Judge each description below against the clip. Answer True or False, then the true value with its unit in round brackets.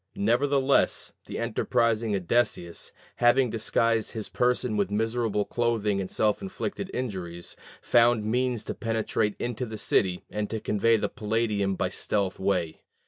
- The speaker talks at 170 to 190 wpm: False (140 wpm)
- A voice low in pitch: True (110 Hz)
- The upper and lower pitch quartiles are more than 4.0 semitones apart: False (2.8 semitones)